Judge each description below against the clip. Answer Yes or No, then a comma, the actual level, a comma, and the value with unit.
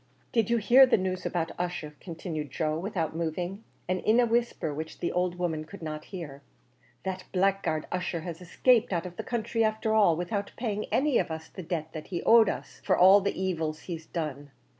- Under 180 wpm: No, fast, 205 wpm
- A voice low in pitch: No, medium, 180 Hz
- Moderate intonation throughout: Yes, average, 4.3 semitones